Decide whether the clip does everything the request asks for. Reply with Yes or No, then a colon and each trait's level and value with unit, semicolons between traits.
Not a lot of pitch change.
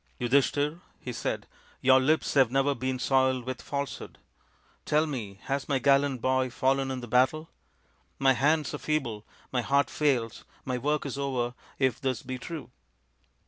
Yes: narrow, 1.9 semitones